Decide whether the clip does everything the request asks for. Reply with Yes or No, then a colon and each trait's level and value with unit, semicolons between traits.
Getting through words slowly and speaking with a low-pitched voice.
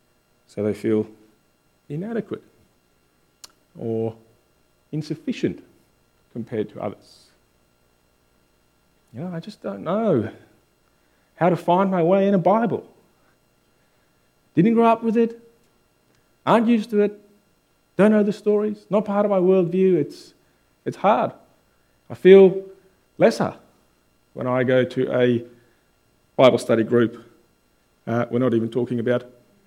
Yes: slow, 125 wpm; low, 120 Hz